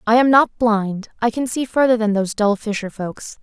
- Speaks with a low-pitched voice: No, high, 225 Hz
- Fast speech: Yes, fast, 210 wpm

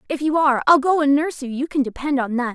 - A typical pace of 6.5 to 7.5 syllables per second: Yes, 6.9 syllables/s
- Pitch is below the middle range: No, very high, 280 Hz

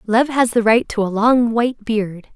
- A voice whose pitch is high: Yes, high, 225 Hz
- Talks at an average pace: No, fast, 230 wpm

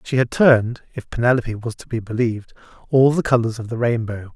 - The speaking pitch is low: Yes, low, 120 Hz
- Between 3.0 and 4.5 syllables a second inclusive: Yes, 4.0 syllables/s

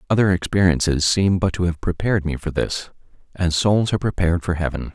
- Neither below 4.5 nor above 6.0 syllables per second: No, 6.3 syllables/s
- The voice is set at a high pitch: No, very low, 90 Hz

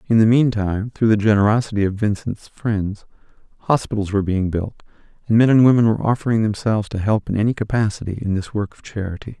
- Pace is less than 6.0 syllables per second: No, 6.5 syllables/s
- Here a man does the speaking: Yes, male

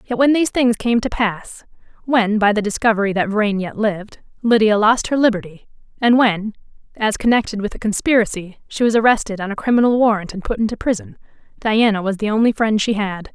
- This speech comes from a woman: Yes, female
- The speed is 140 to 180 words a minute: No, average, 200 wpm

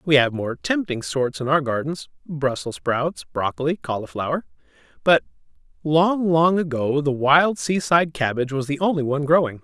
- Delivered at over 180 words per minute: No, average, 150 wpm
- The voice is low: No, medium, 145 Hz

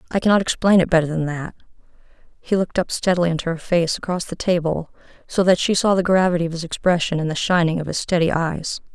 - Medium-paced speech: No, fast, 220 wpm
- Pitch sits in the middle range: Yes, medium, 175 Hz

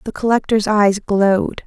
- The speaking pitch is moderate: No, high, 210 Hz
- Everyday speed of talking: Yes, average, 145 wpm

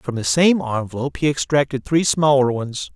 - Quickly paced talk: No, average, 185 wpm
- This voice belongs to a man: Yes, male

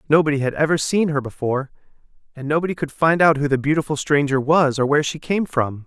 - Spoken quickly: Yes, fast, 215 wpm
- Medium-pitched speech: Yes, medium, 145 Hz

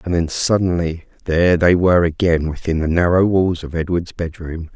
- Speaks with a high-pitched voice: No, very low, 85 Hz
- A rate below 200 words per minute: Yes, average, 175 wpm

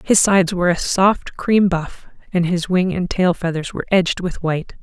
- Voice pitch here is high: No, medium, 180 Hz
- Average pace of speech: No, fast, 210 wpm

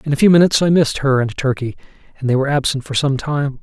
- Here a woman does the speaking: No, male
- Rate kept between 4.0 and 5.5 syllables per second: No, 7.0 syllables/s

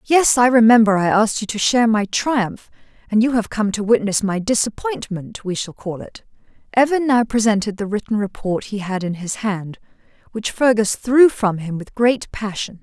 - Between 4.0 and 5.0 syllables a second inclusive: Yes, 4.9 syllables/s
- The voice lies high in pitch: Yes, high, 215 Hz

